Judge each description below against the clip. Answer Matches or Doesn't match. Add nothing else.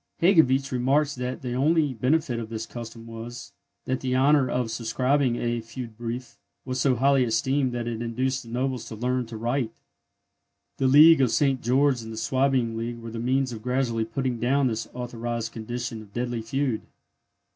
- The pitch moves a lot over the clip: Doesn't match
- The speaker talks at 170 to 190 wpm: Matches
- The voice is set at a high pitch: Doesn't match